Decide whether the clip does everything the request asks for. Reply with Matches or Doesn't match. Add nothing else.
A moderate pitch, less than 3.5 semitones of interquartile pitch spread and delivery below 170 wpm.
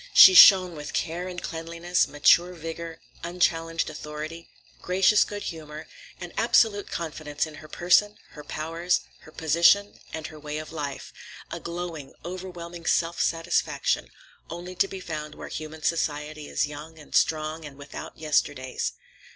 Matches